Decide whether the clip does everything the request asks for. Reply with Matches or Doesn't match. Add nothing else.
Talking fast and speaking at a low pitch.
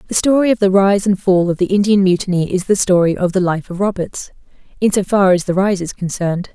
Doesn't match